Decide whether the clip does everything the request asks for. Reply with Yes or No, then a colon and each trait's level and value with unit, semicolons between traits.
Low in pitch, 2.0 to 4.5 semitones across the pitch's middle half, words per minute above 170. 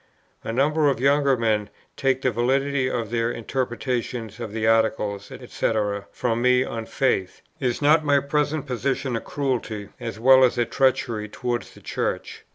No: low, 125 Hz; average, 3.3 semitones; average, 165 wpm